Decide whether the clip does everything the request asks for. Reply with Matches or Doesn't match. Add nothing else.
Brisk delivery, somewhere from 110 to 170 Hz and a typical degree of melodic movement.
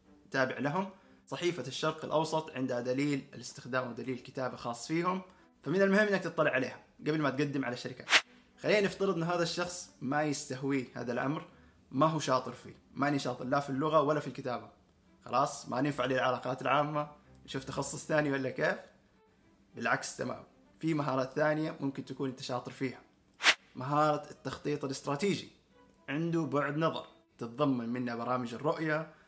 Matches